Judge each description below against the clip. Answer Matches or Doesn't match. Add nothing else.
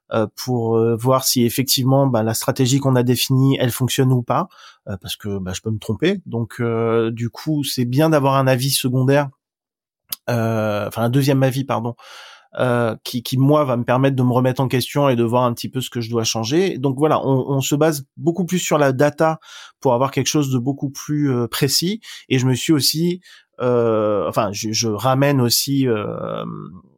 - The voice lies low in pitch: Matches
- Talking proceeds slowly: Doesn't match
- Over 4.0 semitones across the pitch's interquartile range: Doesn't match